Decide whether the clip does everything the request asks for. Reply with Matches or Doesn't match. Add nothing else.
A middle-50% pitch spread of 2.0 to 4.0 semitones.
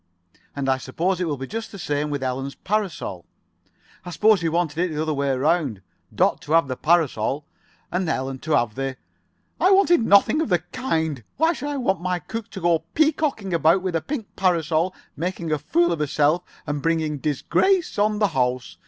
Doesn't match